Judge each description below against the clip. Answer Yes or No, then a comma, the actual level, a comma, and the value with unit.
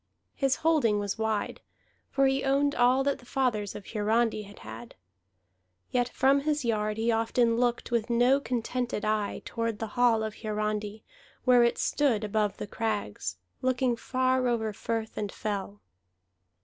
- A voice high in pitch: Yes, high, 230 Hz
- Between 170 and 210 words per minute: No, average, 155 wpm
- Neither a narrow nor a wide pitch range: Yes, average, 3.1 semitones